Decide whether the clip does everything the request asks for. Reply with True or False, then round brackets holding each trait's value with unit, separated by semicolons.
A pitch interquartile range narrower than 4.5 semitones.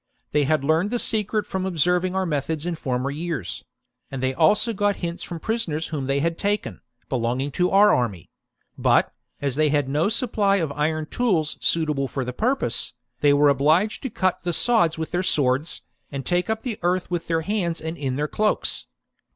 False (5.0 semitones)